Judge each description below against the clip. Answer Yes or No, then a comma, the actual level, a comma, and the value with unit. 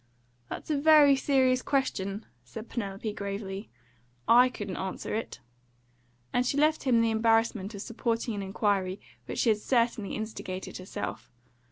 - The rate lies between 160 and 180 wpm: No, average, 145 wpm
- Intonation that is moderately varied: Yes, average, 4.1 semitones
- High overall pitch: Yes, high, 225 Hz